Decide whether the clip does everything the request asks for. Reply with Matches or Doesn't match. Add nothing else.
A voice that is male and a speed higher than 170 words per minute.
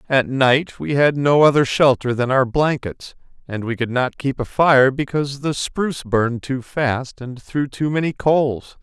Matches